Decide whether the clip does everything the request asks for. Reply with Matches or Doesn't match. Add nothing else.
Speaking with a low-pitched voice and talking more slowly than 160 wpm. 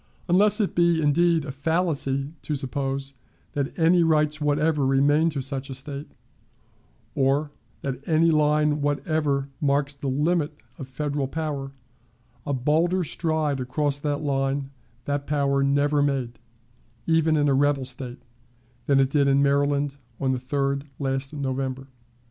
Doesn't match